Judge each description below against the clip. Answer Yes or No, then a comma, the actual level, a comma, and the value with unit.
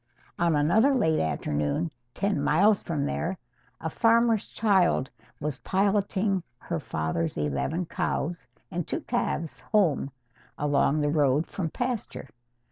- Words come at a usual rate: No, slow, 125 wpm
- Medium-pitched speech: Yes, medium, 165 Hz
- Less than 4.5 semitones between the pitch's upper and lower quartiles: No, wide, 5.6 semitones